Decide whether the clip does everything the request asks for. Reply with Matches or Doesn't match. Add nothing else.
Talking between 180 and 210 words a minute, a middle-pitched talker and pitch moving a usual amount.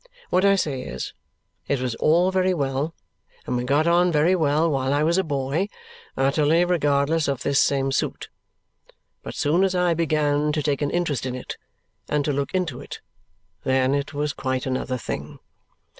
Matches